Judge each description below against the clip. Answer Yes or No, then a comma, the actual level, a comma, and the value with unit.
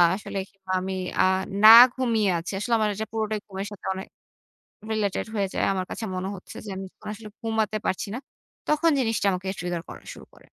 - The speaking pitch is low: No, high, 205 Hz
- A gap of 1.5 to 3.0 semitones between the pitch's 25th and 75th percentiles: Yes, narrow, 2.6 semitones